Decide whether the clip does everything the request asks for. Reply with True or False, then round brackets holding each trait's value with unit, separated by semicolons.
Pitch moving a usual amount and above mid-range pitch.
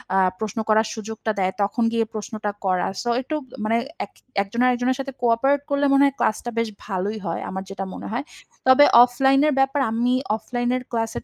True (3.4 semitones; 230 Hz)